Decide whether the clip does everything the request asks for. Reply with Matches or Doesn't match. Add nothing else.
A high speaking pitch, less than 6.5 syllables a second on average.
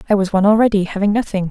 Doesn't match